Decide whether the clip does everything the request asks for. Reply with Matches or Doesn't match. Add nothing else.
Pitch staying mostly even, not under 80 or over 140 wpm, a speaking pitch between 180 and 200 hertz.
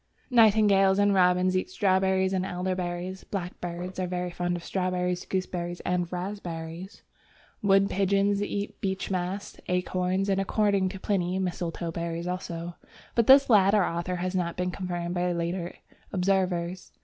Matches